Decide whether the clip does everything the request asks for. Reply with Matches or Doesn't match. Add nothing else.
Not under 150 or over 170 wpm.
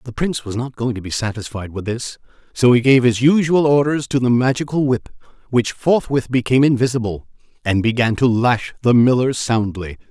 Doesn't match